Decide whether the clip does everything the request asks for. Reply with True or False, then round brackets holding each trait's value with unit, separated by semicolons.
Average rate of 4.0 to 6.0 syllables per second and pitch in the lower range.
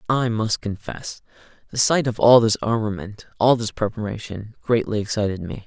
True (5.0 syllables/s; 110 Hz)